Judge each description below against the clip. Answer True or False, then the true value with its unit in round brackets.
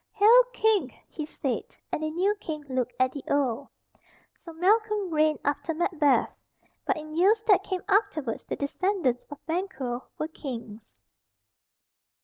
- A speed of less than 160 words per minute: True (140 wpm)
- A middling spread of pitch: False (6.0 semitones)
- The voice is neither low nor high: False (310 Hz)